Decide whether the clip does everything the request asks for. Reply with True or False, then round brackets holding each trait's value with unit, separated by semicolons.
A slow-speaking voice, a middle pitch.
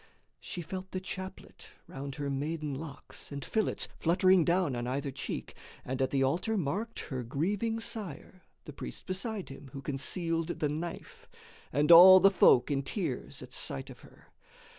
False (165 wpm; 160 Hz)